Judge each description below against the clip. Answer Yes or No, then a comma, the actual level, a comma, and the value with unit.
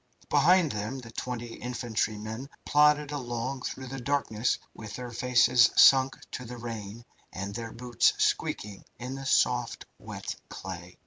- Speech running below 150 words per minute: Yes, average, 140 wpm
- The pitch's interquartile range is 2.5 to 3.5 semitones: Yes, average, 3.2 semitones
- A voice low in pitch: Yes, low, 120 Hz